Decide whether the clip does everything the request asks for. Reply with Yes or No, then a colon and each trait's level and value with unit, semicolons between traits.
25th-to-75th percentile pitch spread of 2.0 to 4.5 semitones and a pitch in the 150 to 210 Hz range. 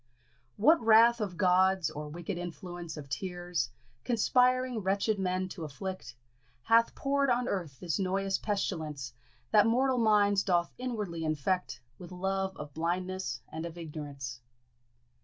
Yes: average, 4.2 semitones; medium, 185 Hz